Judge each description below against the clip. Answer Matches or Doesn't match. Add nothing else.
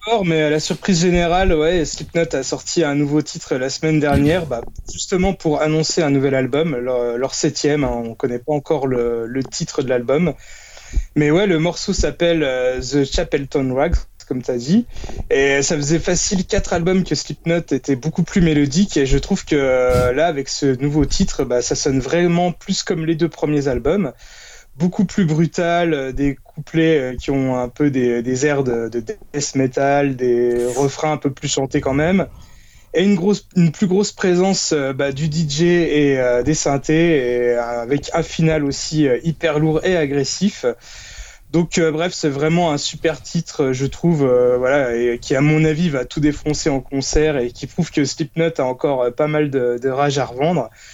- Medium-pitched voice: Matches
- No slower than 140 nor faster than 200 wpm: Matches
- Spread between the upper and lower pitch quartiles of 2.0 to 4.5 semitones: Matches